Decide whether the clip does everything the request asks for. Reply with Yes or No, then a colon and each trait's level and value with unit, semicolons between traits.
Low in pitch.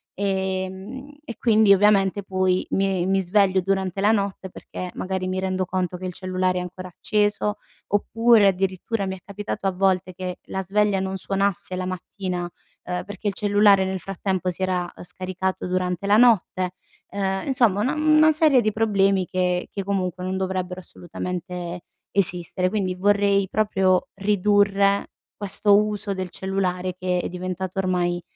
No: high, 190 Hz